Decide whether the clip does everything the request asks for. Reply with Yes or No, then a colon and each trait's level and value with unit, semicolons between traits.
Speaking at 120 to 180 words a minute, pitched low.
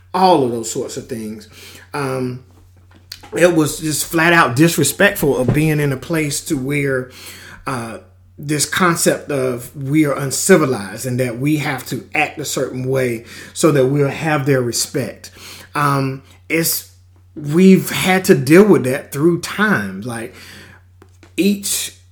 Yes: average, 145 wpm; low, 130 Hz